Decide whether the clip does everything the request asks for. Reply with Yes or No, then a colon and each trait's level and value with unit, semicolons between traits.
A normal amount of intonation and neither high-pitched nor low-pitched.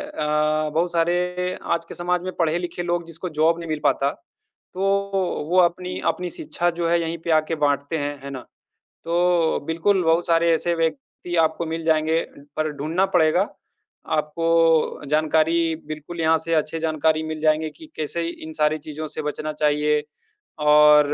No: narrow, 1.9 semitones; medium, 165 Hz